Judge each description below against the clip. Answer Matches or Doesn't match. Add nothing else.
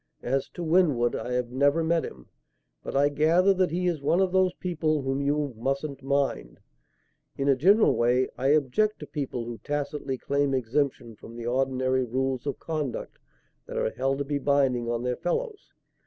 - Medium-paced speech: Matches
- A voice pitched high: Doesn't match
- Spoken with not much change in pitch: Doesn't match